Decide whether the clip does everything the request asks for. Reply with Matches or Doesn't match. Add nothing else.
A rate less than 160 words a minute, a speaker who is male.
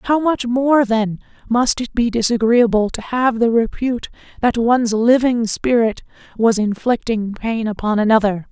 Doesn't match